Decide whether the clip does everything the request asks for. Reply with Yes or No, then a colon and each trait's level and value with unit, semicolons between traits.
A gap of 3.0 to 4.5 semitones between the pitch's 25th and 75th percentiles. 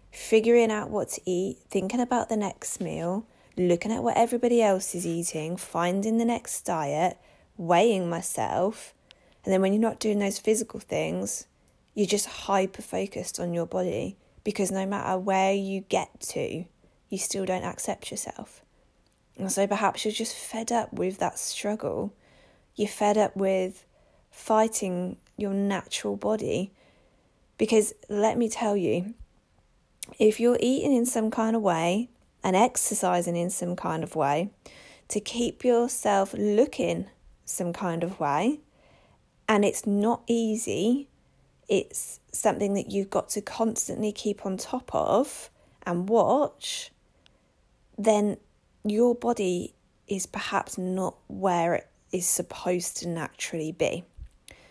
Yes: average, 3.3 semitones